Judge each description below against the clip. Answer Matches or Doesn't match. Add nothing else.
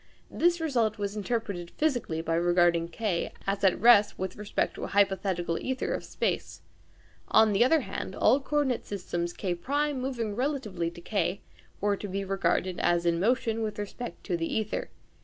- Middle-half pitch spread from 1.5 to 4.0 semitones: Doesn't match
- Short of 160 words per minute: Doesn't match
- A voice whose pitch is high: Matches